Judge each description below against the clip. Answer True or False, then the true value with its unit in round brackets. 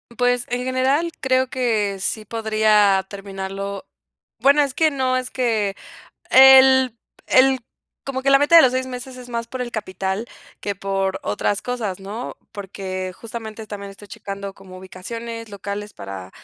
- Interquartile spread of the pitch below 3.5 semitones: False (4.6 semitones)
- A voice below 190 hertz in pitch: False (220 Hz)